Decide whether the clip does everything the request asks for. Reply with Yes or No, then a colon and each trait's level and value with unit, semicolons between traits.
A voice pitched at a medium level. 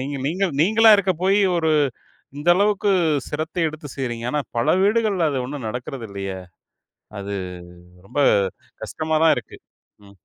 Yes: medium, 155 Hz